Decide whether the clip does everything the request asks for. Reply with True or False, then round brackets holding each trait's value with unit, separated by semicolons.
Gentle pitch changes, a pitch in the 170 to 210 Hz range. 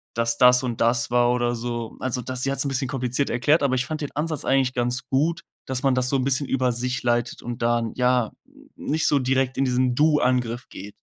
False (1.9 semitones; 125 Hz)